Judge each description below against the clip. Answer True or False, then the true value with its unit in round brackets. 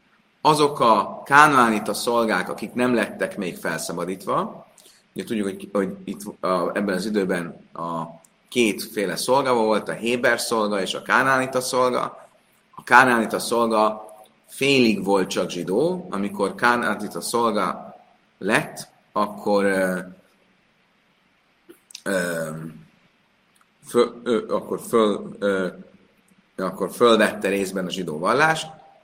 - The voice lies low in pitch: True (110 Hz)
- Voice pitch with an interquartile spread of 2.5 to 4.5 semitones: False (5.1 semitones)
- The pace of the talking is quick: False (110 wpm)